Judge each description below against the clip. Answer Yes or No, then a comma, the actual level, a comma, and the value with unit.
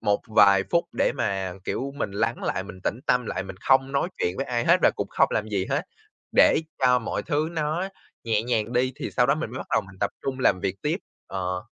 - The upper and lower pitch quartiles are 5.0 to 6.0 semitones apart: Yes, wide, 5.4 semitones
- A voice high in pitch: No, low, 115 Hz